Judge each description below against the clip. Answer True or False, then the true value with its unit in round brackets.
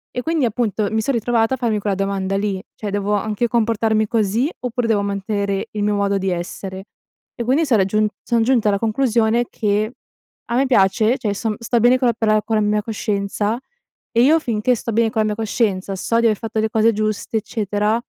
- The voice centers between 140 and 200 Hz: False (220 Hz)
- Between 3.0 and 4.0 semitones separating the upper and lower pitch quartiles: False (2.4 semitones)